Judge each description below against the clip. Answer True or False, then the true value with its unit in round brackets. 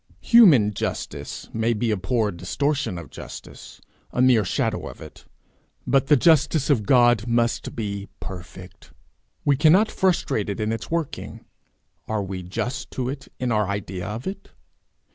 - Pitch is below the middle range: True (115 Hz)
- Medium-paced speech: True (155 wpm)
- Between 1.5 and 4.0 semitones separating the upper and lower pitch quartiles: False (5.5 semitones)